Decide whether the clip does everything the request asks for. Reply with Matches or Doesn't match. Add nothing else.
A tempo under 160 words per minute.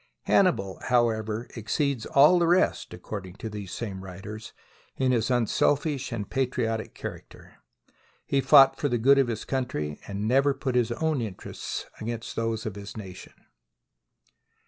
Matches